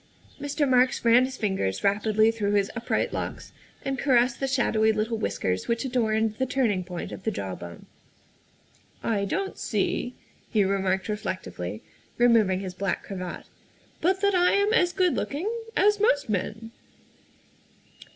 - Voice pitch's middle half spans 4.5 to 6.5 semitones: Yes, average, 5.3 semitones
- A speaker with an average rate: Yes, average, 160 wpm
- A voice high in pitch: Yes, high, 225 Hz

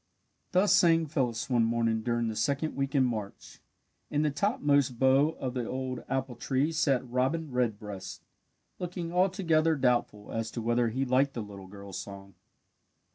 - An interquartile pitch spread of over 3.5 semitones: Yes, average, 4.6 semitones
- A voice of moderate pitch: No, low, 130 Hz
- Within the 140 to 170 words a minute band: Yes, average, 165 wpm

